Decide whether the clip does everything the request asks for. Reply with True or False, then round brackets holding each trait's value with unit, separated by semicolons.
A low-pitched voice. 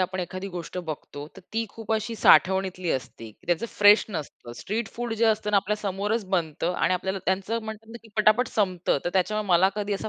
False (195 Hz)